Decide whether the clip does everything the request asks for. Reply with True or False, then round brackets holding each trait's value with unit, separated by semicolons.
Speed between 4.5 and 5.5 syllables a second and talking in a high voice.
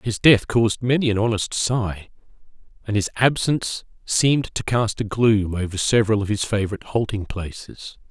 False (5.2 syllables/s; 110 Hz)